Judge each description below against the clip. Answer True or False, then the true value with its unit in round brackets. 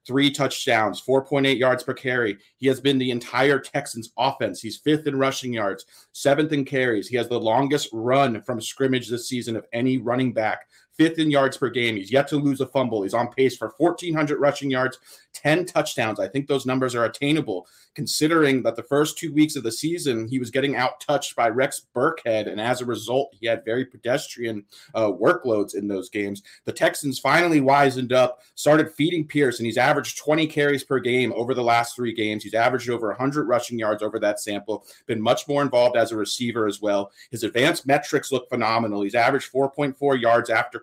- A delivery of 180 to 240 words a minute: True (205 wpm)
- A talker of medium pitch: False (130 Hz)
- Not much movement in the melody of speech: False (3.3 semitones)